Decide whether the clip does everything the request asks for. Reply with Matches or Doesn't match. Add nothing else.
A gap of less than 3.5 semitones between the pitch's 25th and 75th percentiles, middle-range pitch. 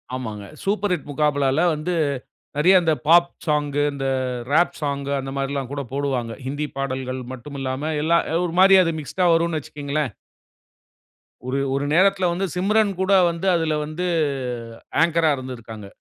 Doesn't match